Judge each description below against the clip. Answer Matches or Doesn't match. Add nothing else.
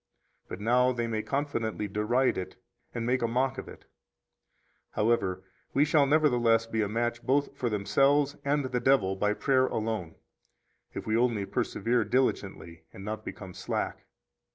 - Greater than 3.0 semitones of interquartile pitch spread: Matches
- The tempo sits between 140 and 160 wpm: Matches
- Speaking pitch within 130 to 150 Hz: Doesn't match